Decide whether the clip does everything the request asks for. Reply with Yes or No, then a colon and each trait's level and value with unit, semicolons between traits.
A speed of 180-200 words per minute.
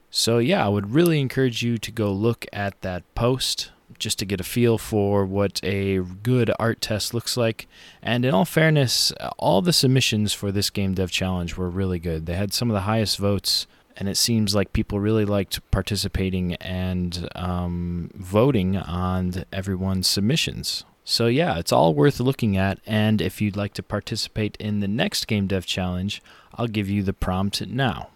Yes: average, 185 wpm